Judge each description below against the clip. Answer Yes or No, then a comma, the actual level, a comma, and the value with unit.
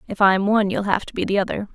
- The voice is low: No, high, 200 Hz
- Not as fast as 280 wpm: No, fast, 310 wpm